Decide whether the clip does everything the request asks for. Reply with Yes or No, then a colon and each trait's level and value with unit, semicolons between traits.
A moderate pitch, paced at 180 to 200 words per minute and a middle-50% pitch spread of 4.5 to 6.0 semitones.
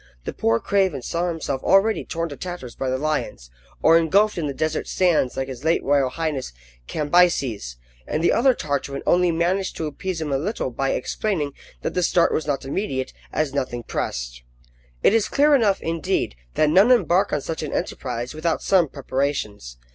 Yes: medium, 155 Hz; average, 185 wpm; average, 5.0 semitones